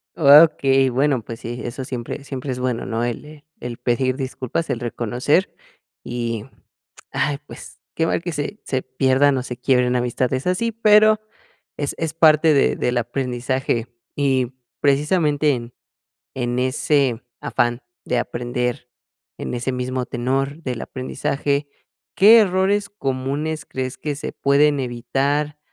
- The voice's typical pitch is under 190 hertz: Yes, low, 135 Hz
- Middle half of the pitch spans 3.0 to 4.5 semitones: Yes, average, 3.3 semitones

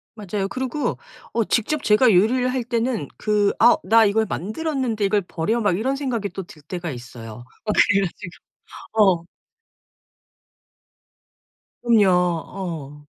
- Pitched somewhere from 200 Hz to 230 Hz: Yes, high, 210 Hz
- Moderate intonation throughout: Yes, average, 4.7 semitones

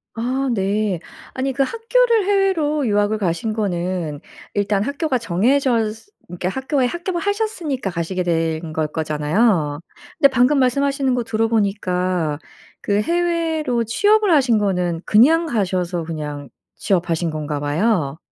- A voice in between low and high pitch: No, high, 215 Hz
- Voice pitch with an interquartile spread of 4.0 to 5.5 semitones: No, wide, 8.2 semitones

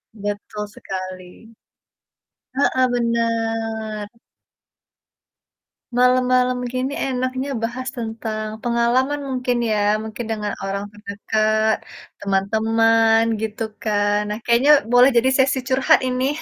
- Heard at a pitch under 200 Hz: No, high, 225 Hz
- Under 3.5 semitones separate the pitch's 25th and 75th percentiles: Yes, average, 2.8 semitones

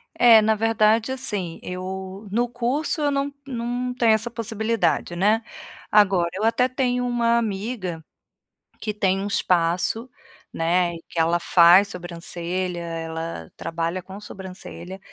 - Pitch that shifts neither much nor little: Yes, average, 4.9 semitones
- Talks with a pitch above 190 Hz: Yes, high, 200 Hz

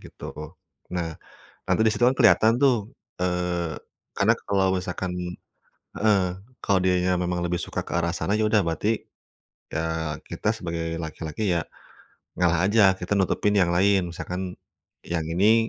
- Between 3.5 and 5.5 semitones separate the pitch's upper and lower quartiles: No, average, 3.1 semitones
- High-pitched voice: No, very low, 90 Hz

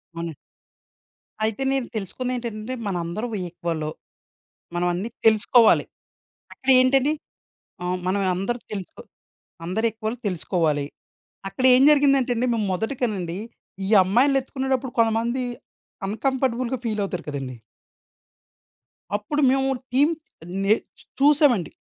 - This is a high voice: Yes, high, 225 Hz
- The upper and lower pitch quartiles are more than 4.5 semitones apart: Yes, wide, 5.6 semitones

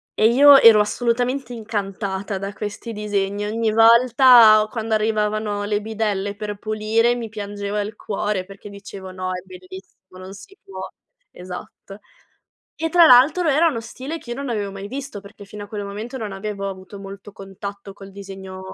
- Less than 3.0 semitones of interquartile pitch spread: Yes, narrow, 2.6 semitones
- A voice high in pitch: Yes, high, 210 Hz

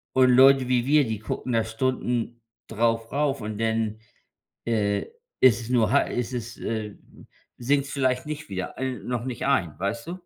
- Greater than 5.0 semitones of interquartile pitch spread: No, average, 2.8 semitones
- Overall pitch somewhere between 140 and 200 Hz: No, low, 120 Hz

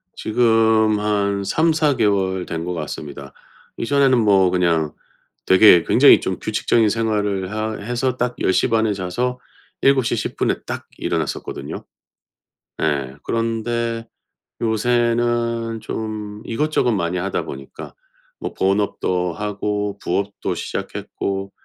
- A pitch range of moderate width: Yes, average, 3.5 semitones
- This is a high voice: No, low, 105 Hz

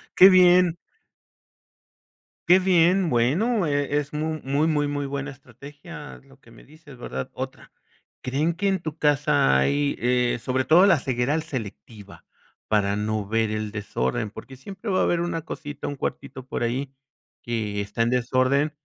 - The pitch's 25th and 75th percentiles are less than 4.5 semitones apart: No, average, 5.2 semitones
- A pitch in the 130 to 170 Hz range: Yes, medium, 140 Hz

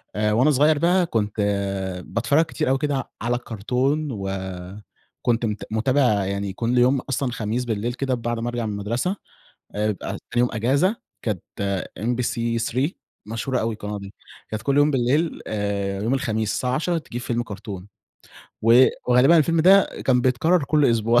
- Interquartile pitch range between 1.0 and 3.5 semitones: No, average, 4.1 semitones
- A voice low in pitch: Yes, low, 120 Hz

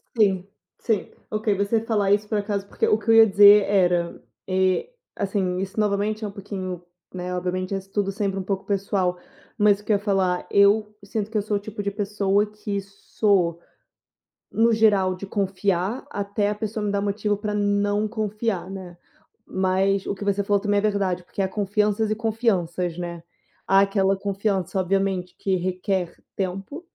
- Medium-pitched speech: No, high, 200 Hz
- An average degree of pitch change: No, narrow, 1.7 semitones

